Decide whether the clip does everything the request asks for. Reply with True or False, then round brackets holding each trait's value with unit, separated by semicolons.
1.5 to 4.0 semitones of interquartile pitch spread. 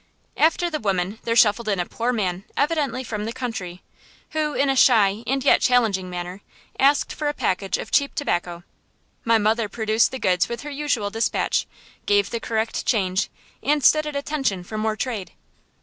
False (5.5 semitones)